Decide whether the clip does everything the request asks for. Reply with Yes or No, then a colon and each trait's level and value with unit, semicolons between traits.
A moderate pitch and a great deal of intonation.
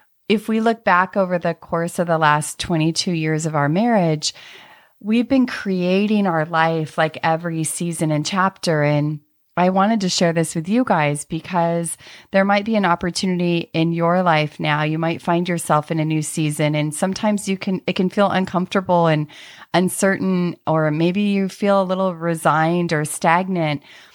No: medium, 170 Hz; average, 3.2 semitones